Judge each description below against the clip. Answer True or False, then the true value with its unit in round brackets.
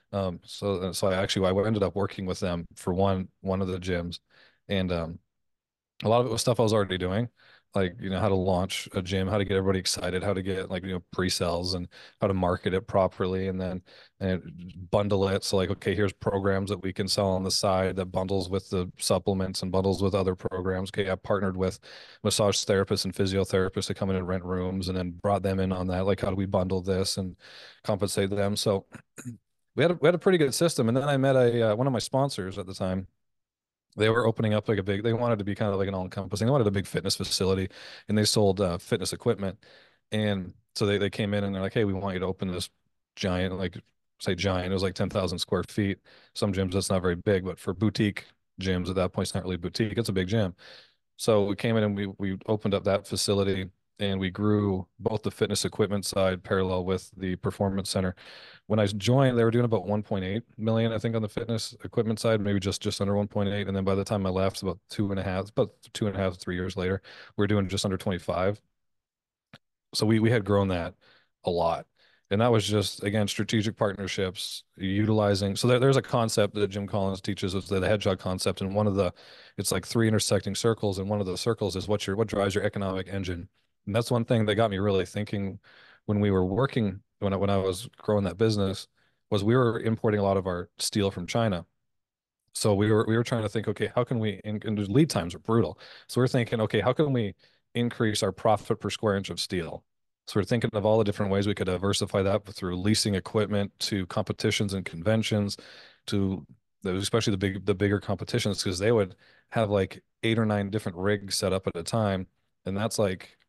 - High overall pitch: False (100 Hz)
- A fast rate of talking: True (235 wpm)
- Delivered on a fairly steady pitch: True (2.3 semitones)